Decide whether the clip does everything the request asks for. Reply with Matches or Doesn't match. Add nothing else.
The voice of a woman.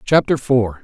Doesn't match